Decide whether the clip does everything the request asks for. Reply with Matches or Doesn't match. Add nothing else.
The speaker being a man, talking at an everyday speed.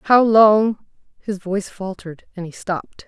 Doesn't match